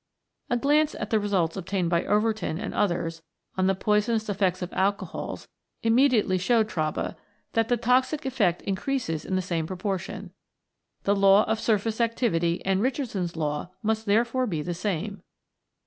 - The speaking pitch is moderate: No, high, 205 Hz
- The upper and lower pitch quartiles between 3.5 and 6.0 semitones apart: Yes, average, 4.0 semitones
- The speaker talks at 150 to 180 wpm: Yes, average, 155 wpm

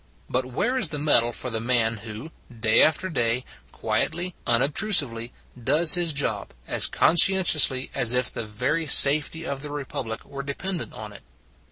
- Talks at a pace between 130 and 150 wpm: No, average, 160 wpm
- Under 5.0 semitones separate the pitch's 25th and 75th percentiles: No, wide, 5.4 semitones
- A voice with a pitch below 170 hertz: Yes, low, 135 Hz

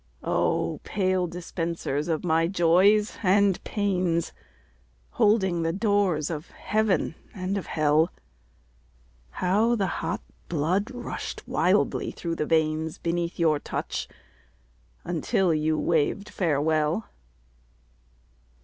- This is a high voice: No, medium, 175 Hz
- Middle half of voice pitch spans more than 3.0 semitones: Yes, average, 3.6 semitones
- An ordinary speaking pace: No, slow, 105 wpm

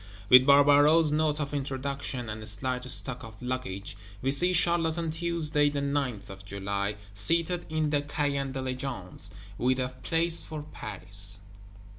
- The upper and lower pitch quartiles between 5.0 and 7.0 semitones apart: Yes, average, 5.3 semitones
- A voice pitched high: No, low, 135 Hz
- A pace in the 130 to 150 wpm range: Yes, average, 145 wpm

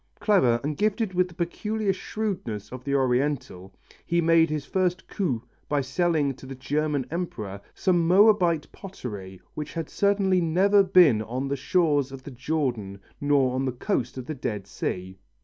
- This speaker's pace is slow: No, average, 165 wpm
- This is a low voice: No, medium, 150 Hz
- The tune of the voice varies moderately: No, wide, 6.1 semitones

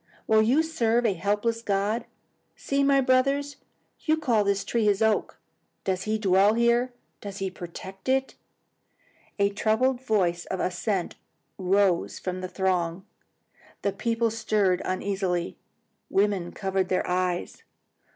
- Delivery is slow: Yes, slow, 130 wpm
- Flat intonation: No, average, 3.8 semitones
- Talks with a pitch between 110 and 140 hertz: No, high, 205 Hz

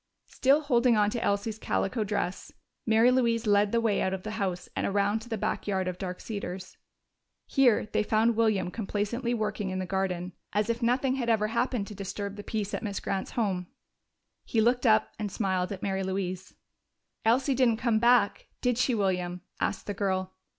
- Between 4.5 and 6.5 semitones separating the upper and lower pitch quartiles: No, average, 3.4 semitones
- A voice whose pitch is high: Yes, high, 210 Hz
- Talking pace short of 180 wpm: No, average, 190 wpm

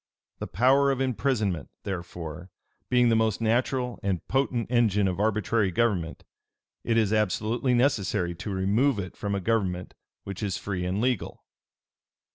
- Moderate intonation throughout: Yes, average, 4.2 semitones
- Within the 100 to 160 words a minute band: Yes, average, 145 wpm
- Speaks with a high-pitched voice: No, low, 105 Hz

